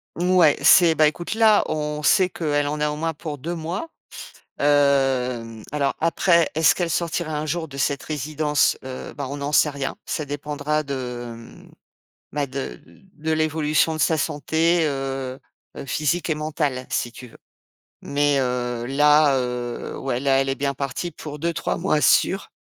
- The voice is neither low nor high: Yes, medium, 150 Hz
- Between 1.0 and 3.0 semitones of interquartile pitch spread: Yes, average, 2.7 semitones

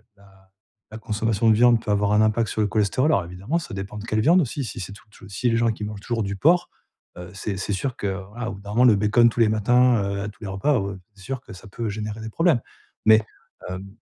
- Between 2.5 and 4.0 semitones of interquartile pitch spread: Yes, average, 3.0 semitones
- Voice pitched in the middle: No, low, 105 Hz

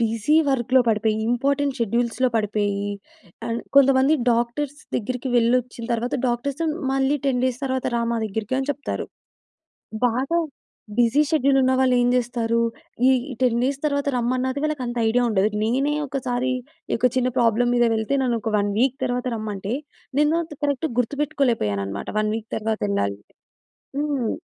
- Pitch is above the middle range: Yes, high, 245 Hz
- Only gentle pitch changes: No, average, 3.0 semitones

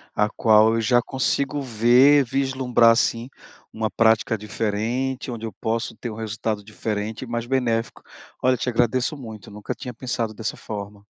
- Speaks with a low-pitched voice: Yes, low, 115 Hz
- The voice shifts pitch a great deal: No, average, 2.7 semitones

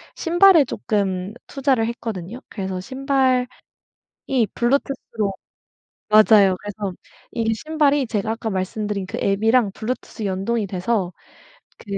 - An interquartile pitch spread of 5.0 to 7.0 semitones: No, average, 4.5 semitones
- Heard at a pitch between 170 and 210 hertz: No, high, 220 Hz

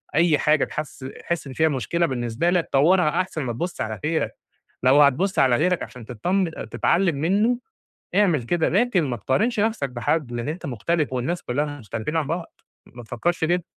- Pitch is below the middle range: No, medium, 155 Hz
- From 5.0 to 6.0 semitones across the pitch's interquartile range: Yes, average, 5.3 semitones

